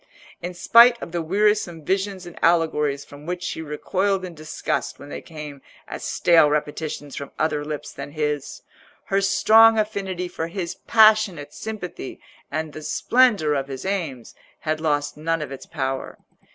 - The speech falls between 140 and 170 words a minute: Yes, average, 160 wpm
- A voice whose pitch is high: No, medium, 165 Hz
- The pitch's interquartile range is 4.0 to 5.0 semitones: Yes, average, 4.6 semitones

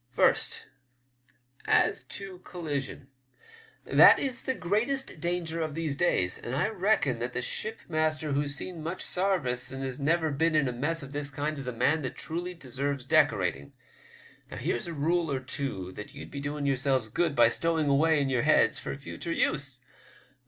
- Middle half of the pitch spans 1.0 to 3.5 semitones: No, average, 3.9 semitones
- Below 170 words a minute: No, average, 175 wpm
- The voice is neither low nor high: Yes, medium, 150 Hz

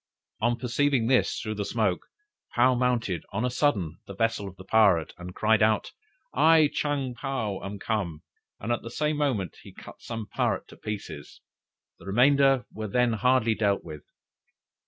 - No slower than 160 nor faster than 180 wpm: Yes, average, 170 wpm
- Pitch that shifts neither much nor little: Yes, average, 4.2 semitones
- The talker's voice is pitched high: No, low, 115 Hz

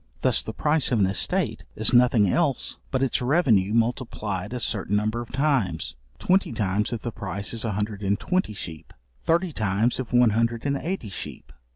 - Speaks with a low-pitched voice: Yes, low, 115 Hz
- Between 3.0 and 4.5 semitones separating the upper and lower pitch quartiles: Yes, average, 4.1 semitones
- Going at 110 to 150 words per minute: No, average, 190 wpm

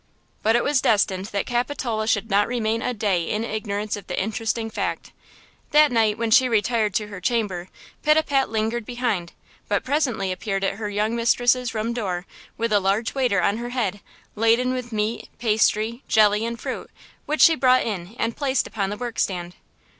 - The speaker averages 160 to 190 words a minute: Yes, average, 185 wpm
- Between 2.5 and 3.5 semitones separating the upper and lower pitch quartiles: Yes, average, 2.9 semitones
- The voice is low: No, high, 220 Hz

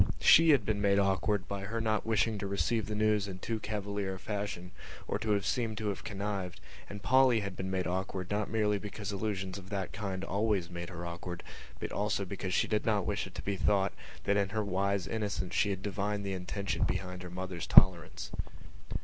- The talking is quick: Yes, fast, 210 wpm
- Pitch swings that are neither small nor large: No, narrow, 2.0 semitones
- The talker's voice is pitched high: No, low, 100 Hz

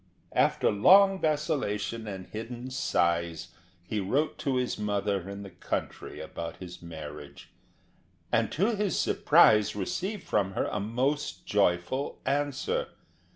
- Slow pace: Yes, slow, 125 wpm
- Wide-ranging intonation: Yes, wide, 7.3 semitones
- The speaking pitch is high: No, low, 105 Hz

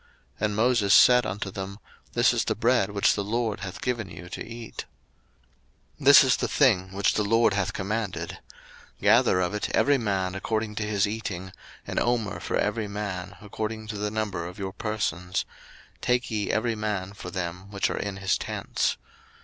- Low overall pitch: Yes, low, 105 Hz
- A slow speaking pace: No, average, 180 wpm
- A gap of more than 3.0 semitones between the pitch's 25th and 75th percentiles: No, average, 2.7 semitones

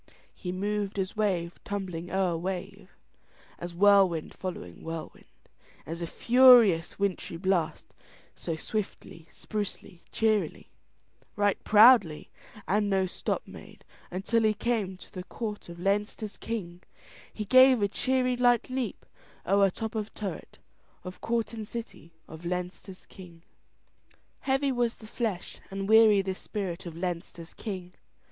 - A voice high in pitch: Yes, high, 195 Hz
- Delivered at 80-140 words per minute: Yes, slow, 135 wpm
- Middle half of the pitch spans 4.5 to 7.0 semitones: No, average, 3.6 semitones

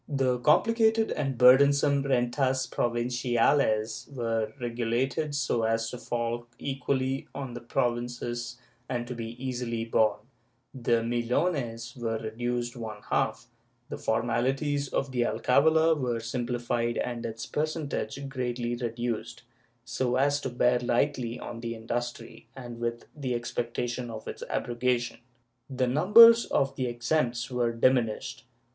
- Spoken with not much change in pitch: Yes, narrow, 2.2 semitones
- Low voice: Yes, low, 120 Hz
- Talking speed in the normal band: No, slow, 130 wpm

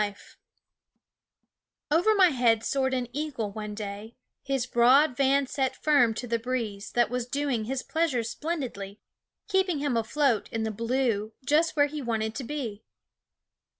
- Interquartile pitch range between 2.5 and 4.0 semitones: No, average, 4.4 semitones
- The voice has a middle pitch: No, very high, 250 Hz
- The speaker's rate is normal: Yes, average, 150 wpm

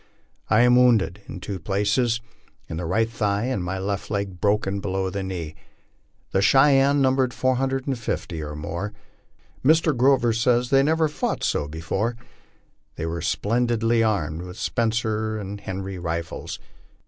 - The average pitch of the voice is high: No, low, 105 Hz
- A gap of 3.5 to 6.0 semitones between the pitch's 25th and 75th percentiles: Yes, average, 4.6 semitones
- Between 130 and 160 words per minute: Yes, average, 150 wpm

